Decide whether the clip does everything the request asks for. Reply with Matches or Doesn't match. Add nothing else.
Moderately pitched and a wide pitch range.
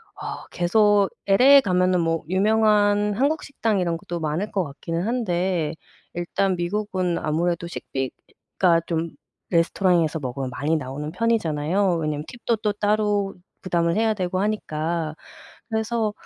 Doesn't match